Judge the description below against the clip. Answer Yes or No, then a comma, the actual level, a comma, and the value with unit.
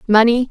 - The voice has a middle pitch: No, high, 230 Hz